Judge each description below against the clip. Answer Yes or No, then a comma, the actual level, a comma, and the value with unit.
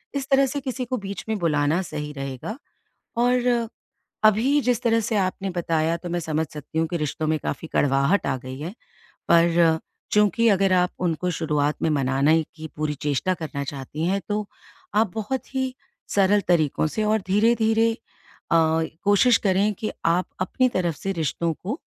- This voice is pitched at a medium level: Yes, medium, 175 Hz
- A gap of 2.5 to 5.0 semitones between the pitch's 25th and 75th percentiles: No, wide, 5.5 semitones